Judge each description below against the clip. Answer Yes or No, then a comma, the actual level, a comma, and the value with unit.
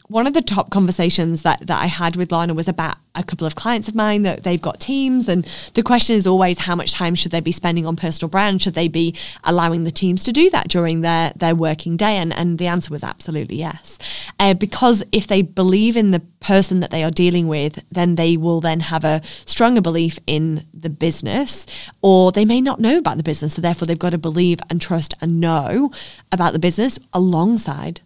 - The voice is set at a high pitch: No, medium, 175 Hz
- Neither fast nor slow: No, fast, 225 wpm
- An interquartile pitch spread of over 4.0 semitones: No, average, 2.9 semitones